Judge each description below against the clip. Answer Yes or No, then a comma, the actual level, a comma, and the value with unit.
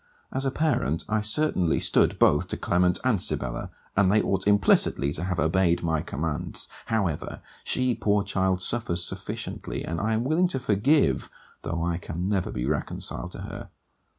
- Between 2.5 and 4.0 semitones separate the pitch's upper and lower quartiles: No, average, 4.8 semitones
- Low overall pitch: Yes, very low, 95 Hz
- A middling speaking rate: Yes, average, 170 wpm